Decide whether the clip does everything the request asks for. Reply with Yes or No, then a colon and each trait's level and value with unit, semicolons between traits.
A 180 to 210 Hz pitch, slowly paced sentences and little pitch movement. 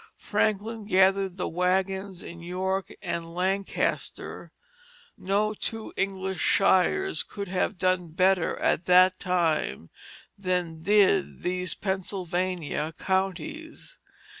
Yes: medium, 185 Hz; slow, 100 wpm; narrow, 1.6 semitones